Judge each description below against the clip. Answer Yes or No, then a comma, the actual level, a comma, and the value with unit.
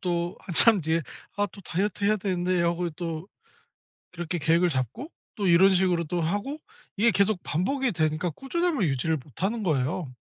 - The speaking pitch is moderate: Yes, medium, 180 Hz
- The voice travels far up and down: No, average, 3.8 semitones